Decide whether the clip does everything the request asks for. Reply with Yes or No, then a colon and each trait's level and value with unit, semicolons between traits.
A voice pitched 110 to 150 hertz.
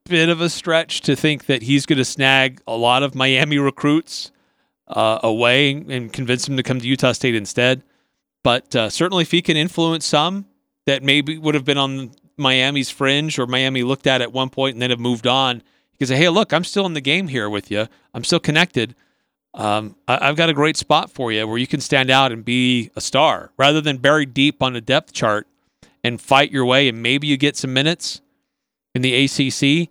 Yes: low, 135 Hz